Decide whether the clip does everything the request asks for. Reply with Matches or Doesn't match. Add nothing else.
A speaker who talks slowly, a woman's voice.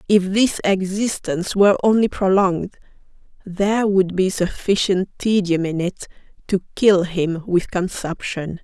Matches